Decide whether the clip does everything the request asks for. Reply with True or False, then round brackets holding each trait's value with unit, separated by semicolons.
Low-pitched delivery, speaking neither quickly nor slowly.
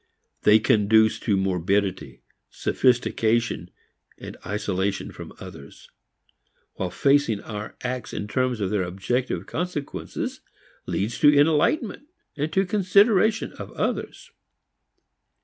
False (115 Hz; 100 wpm)